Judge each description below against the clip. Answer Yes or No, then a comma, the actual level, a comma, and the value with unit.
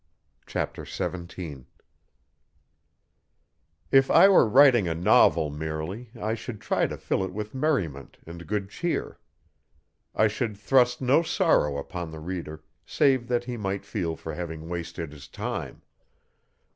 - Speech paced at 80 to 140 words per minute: Yes, slow, 135 wpm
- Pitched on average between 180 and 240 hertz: No, very low, 95 Hz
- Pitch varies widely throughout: Yes, wide, 7.0 semitones